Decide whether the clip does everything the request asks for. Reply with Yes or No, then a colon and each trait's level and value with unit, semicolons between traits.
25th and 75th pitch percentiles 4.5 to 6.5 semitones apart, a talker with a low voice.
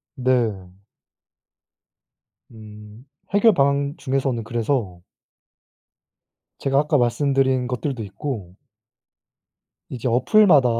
No: average, 3.9 semitones; low, 130 Hz